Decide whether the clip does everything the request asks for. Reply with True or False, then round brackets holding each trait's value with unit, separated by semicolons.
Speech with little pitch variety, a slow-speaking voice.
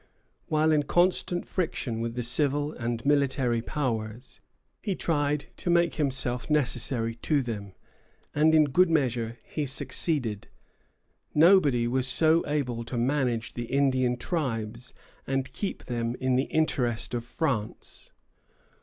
False (4.2 semitones; 130 wpm)